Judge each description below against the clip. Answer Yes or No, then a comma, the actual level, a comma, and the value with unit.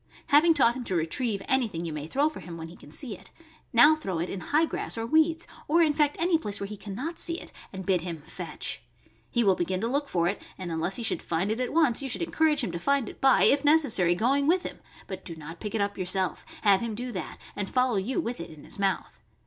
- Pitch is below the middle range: No, high, 225 Hz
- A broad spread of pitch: Yes, wide, 7.5 semitones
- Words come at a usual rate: No, fast, 265 wpm